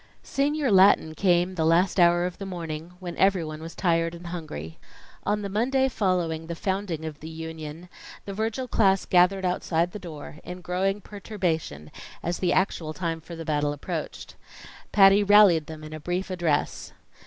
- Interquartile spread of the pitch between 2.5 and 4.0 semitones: Yes, average, 3.3 semitones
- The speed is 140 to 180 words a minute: Yes, average, 170 wpm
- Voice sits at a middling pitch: Yes, medium, 175 Hz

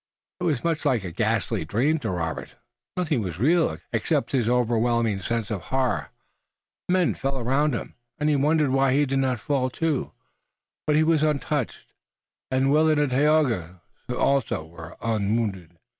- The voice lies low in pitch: Yes, low, 130 Hz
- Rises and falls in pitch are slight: No, average, 5.2 semitones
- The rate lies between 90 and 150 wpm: No, average, 160 wpm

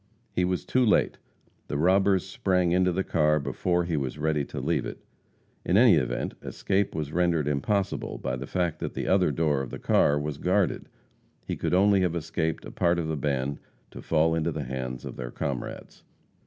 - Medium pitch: No, very low, 80 Hz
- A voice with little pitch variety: No, average, 4.0 semitones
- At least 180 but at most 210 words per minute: Yes, average, 195 wpm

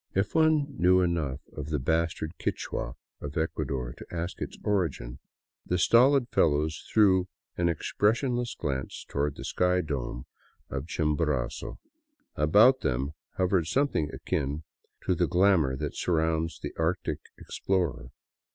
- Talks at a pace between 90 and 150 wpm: Yes, slow, 135 wpm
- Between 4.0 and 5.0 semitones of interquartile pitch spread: Yes, average, 4.3 semitones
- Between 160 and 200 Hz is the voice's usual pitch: No, very low, 80 Hz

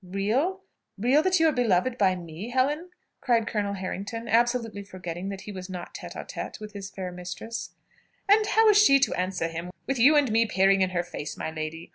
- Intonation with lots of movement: Yes, wide, 5.8 semitones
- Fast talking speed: Yes, fast, 210 wpm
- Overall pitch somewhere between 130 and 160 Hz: No, high, 210 Hz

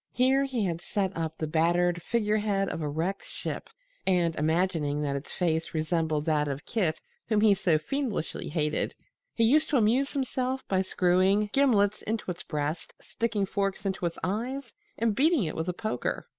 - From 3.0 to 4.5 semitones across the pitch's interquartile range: No, wide, 5.5 semitones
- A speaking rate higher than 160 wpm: Yes, average, 175 wpm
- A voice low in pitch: No, high, 190 Hz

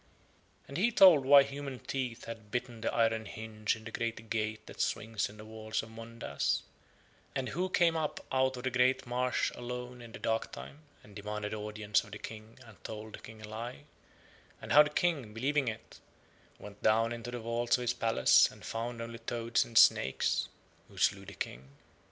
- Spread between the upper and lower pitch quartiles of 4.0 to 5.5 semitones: No, narrow, 2.5 semitones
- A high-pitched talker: No, low, 115 Hz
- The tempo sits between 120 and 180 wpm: No, average, 190 wpm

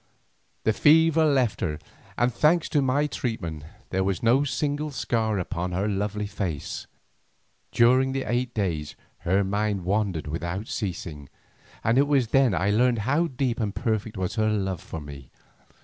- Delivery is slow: No, average, 155 wpm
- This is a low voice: Yes, low, 110 Hz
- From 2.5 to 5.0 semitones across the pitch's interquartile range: No, wide, 5.6 semitones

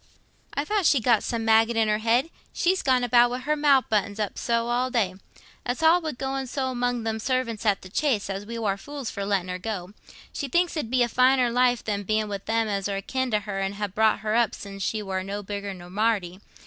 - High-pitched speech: Yes, high, 225 Hz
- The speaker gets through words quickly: Yes, fast, 240 wpm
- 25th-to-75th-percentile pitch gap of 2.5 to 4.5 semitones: Yes, average, 3.9 semitones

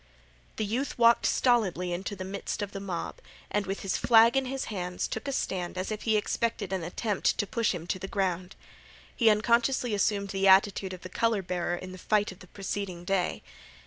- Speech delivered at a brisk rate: Yes, fast, 210 wpm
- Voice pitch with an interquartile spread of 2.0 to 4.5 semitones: Yes, average, 3.3 semitones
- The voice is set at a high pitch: Yes, high, 200 Hz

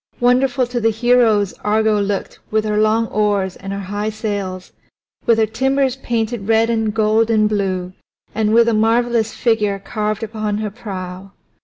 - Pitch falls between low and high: No, high, 215 Hz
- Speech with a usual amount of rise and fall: No, narrow, 2.0 semitones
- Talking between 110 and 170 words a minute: Yes, average, 165 wpm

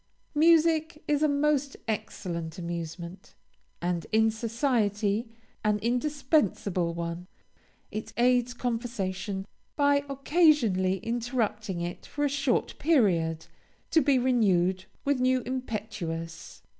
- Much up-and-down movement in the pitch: Yes, wide, 6.8 semitones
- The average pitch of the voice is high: Yes, high, 225 Hz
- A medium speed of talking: No, slow, 105 wpm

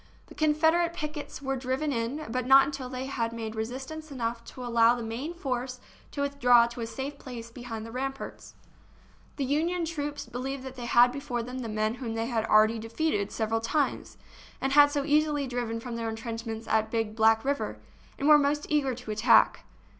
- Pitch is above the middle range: Yes, very high, 250 Hz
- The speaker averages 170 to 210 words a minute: Yes, average, 190 wpm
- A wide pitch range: No, average, 3.7 semitones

